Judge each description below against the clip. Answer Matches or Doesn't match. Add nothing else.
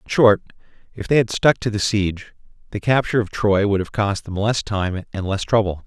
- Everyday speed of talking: Doesn't match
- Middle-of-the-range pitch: Doesn't match